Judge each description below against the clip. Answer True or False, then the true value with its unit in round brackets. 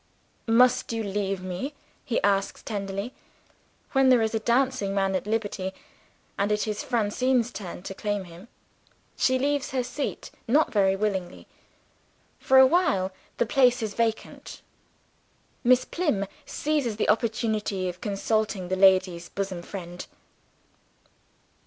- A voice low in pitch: False (210 Hz)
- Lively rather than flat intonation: False (4.3 semitones)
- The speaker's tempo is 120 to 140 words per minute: True (135 wpm)